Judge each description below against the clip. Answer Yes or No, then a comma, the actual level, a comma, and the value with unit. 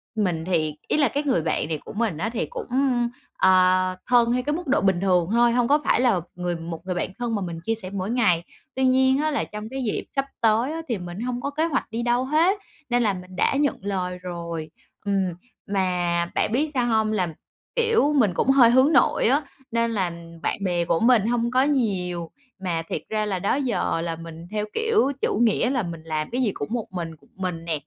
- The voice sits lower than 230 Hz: Yes, high, 215 Hz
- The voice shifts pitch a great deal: Yes, wide, 6.1 semitones